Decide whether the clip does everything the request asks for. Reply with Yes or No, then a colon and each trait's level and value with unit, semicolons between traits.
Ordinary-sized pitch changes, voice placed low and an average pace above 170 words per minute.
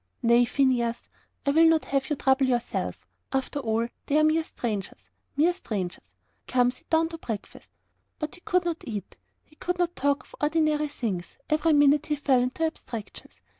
No: average, 4.8 semitones; very high, 280 Hz; average, 180 wpm